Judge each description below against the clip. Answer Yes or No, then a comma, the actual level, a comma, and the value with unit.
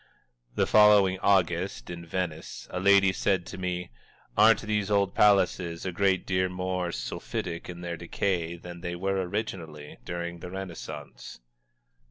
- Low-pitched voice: Yes, very low, 90 Hz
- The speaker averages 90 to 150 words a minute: Yes, average, 145 wpm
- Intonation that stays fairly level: Yes, narrow, 2.3 semitones